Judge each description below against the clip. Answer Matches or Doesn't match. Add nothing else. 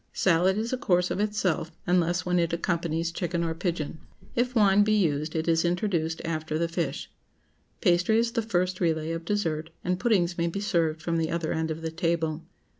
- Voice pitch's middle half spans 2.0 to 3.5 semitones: Matches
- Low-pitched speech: Doesn't match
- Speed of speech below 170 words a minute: Doesn't match